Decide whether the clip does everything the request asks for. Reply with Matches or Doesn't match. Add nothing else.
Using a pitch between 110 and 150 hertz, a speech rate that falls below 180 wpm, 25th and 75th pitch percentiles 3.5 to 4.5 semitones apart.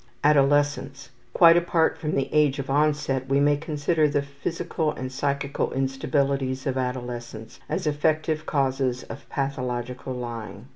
Doesn't match